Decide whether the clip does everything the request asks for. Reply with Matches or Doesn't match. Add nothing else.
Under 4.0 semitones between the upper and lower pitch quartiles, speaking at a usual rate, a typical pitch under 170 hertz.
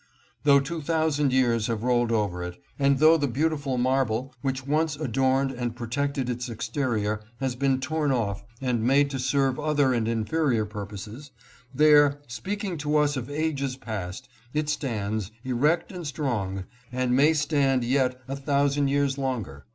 Matches